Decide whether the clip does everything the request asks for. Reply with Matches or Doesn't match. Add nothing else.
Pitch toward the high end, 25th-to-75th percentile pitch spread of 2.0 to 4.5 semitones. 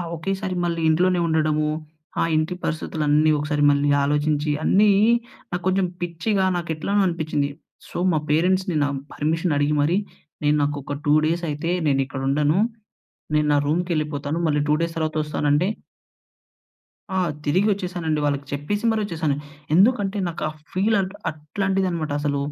Doesn't match